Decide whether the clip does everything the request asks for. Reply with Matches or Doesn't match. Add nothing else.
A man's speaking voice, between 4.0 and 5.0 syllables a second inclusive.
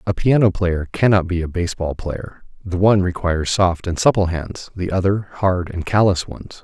Matches